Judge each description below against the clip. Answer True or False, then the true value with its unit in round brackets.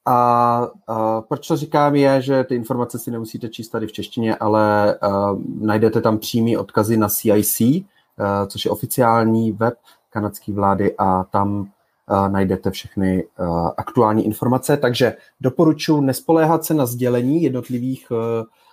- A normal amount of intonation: True (3.5 semitones)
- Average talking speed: True (145 wpm)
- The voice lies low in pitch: True (115 Hz)